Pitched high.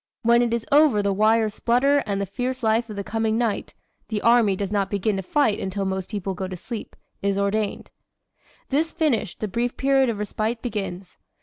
Yes: high, 215 Hz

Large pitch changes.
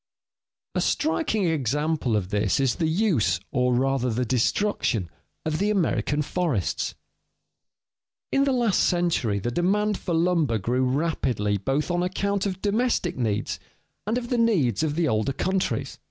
Yes: wide, 7.9 semitones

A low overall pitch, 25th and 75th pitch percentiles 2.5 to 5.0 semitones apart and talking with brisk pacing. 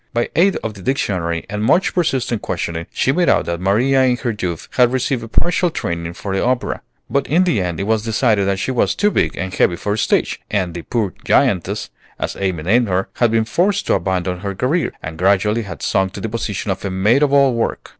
No: low, 105 Hz; wide, 5.4 semitones; fast, 235 wpm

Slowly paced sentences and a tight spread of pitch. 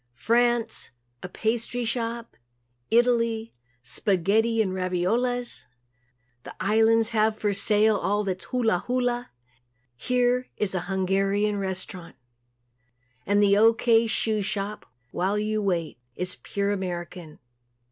No: slow, 115 wpm; average, 3.2 semitones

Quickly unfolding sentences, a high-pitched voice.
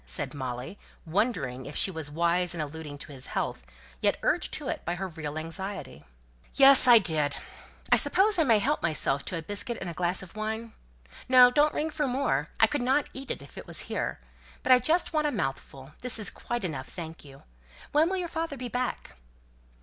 Yes: fast, 210 wpm; high, 195 Hz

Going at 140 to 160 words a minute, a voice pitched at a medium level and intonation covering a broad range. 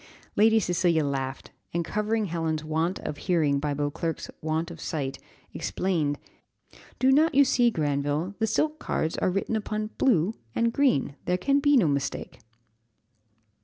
Yes: average, 150 wpm; medium, 170 Hz; wide, 6.6 semitones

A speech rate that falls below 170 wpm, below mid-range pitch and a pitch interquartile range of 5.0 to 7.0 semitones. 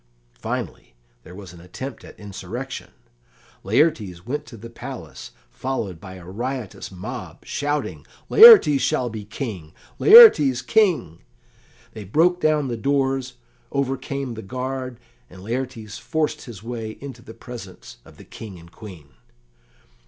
Yes: slow, 135 wpm; low, 120 Hz; wide, 5.6 semitones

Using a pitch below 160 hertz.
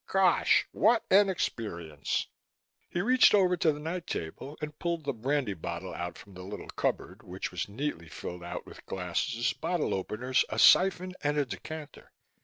Yes: medium, 140 Hz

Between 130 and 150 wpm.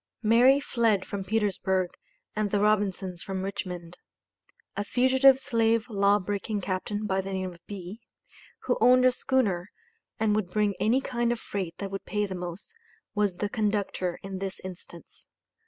No: average, 160 wpm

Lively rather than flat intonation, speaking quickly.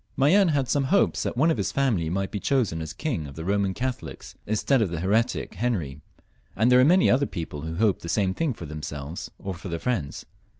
Yes: wide, 7.8 semitones; fast, 220 wpm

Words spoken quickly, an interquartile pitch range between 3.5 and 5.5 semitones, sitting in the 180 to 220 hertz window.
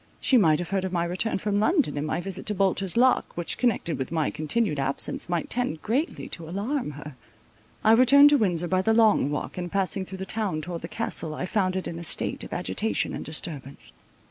Yes: fast, 220 wpm; average, 5.1 semitones; medium, 185 Hz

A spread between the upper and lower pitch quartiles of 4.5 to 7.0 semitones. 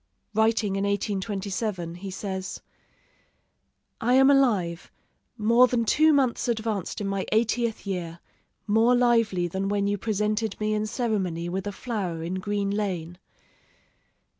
No: average, 3.2 semitones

